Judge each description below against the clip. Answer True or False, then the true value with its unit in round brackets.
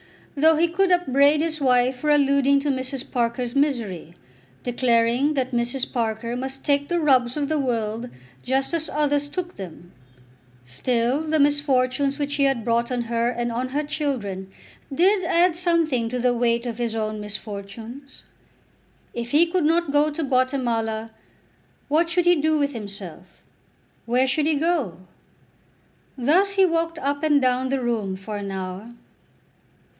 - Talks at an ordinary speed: True (160 wpm)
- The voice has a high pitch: True (260 Hz)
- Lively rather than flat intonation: False (4.3 semitones)